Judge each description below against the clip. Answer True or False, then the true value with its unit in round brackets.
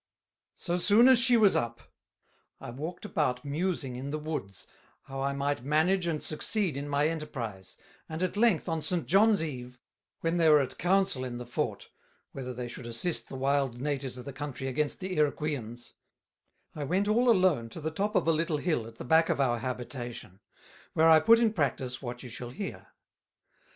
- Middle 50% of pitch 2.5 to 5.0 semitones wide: False (5.6 semitones)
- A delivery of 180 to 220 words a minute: True (190 wpm)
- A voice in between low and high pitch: True (150 Hz)